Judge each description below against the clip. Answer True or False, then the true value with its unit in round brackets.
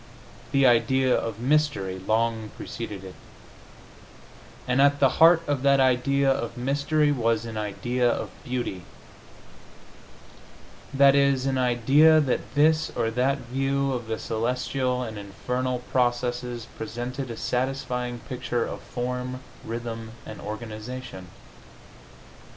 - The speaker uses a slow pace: True (120 wpm)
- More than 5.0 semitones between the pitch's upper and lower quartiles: False (2.7 semitones)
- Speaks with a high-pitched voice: False (125 Hz)